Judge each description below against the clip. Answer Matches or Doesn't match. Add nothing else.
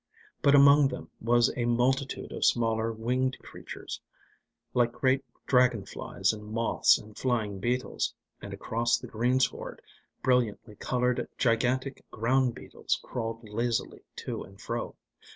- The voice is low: Matches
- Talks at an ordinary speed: Doesn't match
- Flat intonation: Matches